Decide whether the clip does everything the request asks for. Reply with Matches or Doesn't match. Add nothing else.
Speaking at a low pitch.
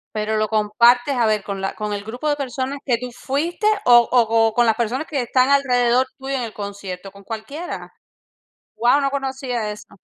Doesn't match